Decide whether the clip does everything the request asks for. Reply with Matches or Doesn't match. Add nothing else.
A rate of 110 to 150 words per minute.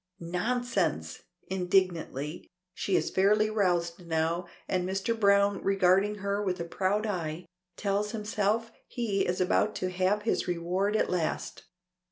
Matches